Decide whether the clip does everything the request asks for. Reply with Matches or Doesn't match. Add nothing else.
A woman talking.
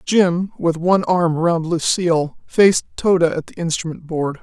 Matches